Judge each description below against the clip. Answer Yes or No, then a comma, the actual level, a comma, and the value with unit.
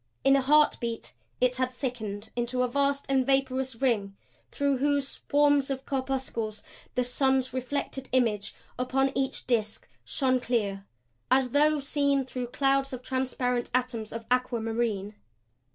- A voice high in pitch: Yes, very high, 255 Hz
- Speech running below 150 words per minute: Yes, average, 140 wpm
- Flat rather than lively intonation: Yes, narrow, 2.3 semitones